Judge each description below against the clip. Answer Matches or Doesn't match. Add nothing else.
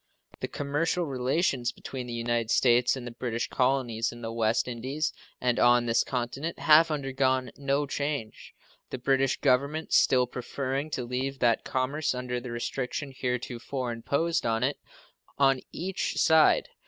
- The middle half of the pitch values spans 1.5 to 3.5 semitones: Matches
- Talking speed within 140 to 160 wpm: Matches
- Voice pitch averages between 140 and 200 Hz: Doesn't match